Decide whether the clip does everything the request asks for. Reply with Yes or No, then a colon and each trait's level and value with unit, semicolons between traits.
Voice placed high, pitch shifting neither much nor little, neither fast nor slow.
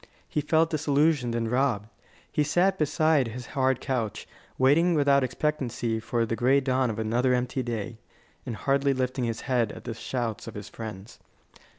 No: low, 130 Hz; average, 3.5 semitones; average, 170 wpm